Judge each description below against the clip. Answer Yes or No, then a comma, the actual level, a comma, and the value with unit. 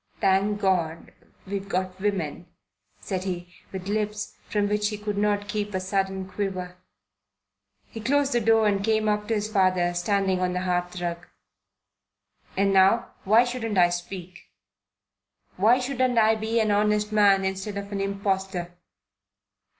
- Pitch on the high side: Yes, high, 200 Hz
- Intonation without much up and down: Yes, narrow, 2.3 semitones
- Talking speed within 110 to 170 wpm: Yes, average, 150 wpm